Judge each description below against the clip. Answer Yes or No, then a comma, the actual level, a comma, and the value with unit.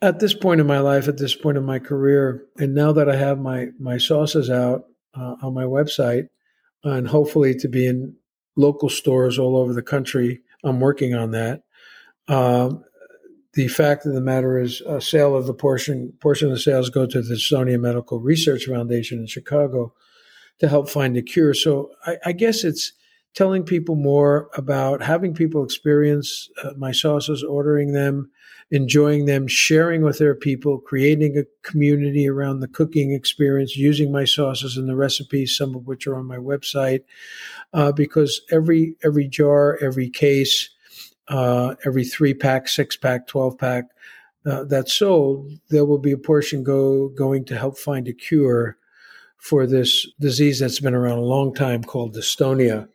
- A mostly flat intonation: Yes, narrow, 2.2 semitones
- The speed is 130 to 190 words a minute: Yes, average, 175 wpm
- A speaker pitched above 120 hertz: Yes, medium, 140 Hz